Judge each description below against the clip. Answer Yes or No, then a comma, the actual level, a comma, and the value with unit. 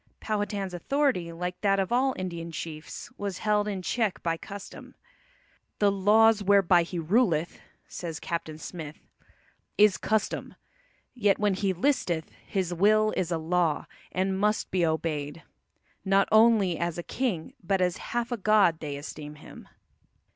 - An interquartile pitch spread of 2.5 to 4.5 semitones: Yes, average, 3.8 semitones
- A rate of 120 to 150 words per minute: Yes, average, 145 wpm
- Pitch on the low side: No, high, 190 Hz